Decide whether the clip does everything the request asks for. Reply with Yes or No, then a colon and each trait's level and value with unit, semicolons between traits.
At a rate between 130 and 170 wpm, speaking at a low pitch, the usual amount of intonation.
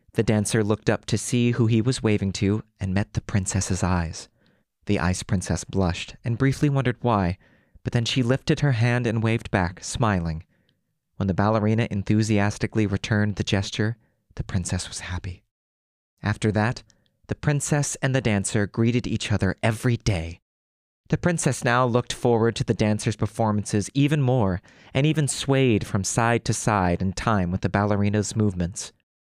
Yes: average, 165 wpm; low, 110 Hz; average, 3.6 semitones